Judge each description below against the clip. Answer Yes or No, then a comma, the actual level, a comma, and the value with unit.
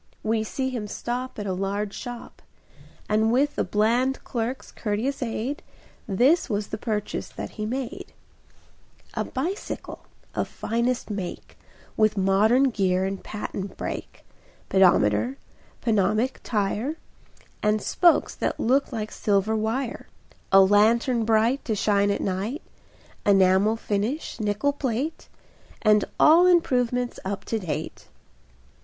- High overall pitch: Yes, high, 220 Hz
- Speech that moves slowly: Yes, slow, 125 wpm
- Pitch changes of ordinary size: Yes, average, 3.8 semitones